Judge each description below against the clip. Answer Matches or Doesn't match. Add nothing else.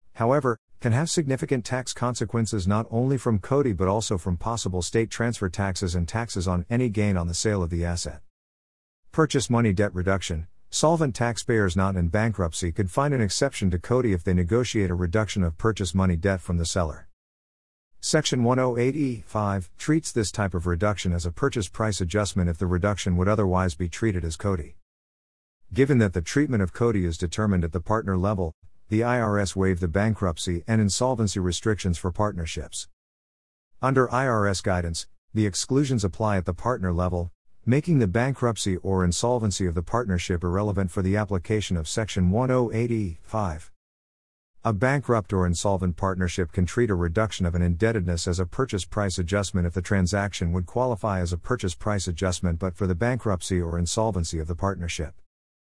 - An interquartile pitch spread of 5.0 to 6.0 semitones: Doesn't match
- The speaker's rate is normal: Matches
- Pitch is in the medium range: Doesn't match